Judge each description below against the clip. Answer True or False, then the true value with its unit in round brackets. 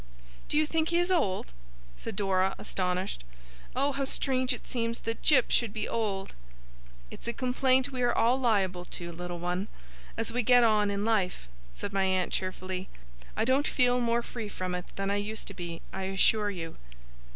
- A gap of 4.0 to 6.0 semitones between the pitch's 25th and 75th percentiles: True (5.0 semitones)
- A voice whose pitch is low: False (210 Hz)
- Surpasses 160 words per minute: True (185 wpm)